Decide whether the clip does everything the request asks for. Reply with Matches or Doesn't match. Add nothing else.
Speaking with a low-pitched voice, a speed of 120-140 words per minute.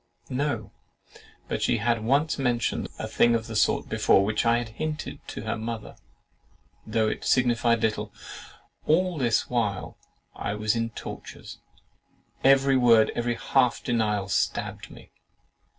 Matches